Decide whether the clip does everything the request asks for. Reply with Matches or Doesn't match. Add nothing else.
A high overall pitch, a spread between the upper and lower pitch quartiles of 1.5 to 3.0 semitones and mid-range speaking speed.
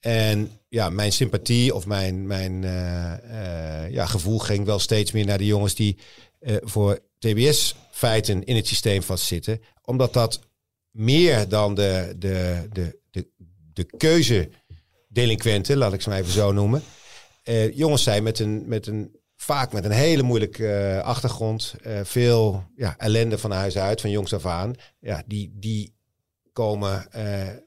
Doesn't match